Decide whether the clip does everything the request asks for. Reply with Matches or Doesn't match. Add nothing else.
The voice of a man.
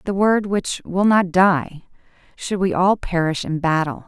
Doesn't match